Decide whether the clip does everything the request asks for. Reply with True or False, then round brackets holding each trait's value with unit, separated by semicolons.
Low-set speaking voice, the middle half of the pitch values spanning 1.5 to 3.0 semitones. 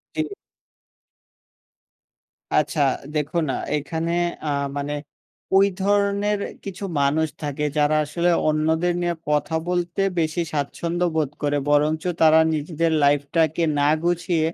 False (160 Hz; 2.7 semitones)